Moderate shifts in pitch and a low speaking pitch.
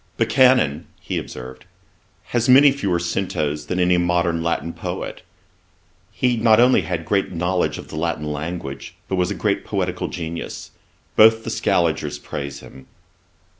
No: wide, 6.0 semitones; very low, 85 Hz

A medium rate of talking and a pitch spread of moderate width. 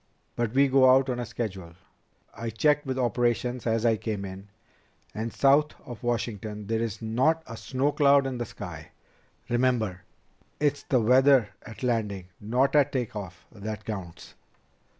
Yes: average, 150 wpm; average, 3.5 semitones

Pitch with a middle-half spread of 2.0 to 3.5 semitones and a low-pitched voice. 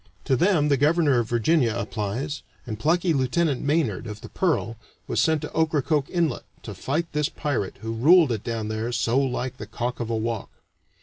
No: average, 5.3 semitones; low, 130 Hz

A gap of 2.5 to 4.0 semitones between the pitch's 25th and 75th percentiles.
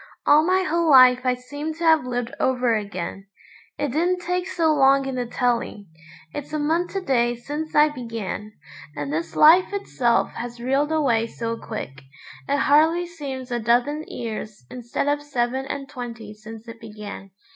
No: average, 4.7 semitones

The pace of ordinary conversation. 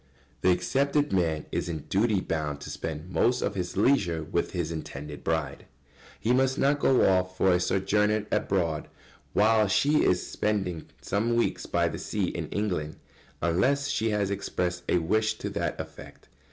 Yes: average, 170 wpm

